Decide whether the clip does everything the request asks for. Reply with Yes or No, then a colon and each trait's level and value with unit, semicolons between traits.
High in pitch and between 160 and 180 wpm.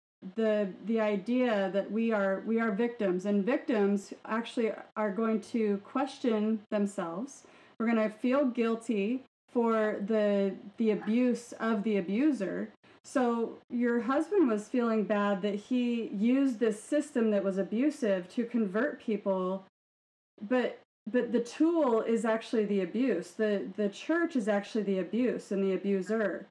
No: high, 220 Hz; average, 145 wpm